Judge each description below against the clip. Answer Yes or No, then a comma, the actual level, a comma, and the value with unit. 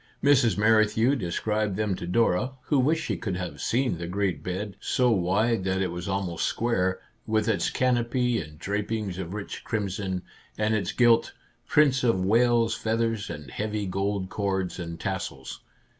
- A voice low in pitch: Yes, low, 105 Hz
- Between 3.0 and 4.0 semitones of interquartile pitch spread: Yes, average, 3.7 semitones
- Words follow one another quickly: No, average, 165 wpm